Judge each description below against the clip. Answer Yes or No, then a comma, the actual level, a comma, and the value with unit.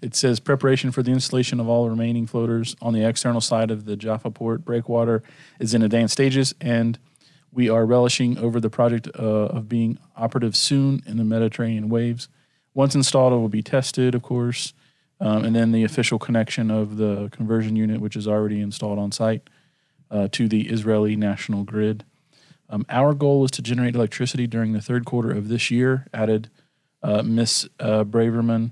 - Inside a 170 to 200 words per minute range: Yes, average, 185 wpm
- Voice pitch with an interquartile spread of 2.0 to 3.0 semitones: Yes, average, 2.7 semitones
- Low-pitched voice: Yes, low, 115 Hz